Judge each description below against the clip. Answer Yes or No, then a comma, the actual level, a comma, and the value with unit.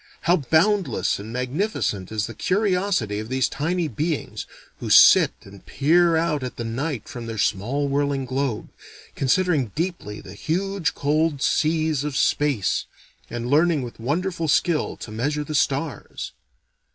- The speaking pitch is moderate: Yes, medium, 145 Hz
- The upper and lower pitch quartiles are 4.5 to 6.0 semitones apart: Yes, wide, 5.5 semitones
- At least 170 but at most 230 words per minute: No, average, 145 wpm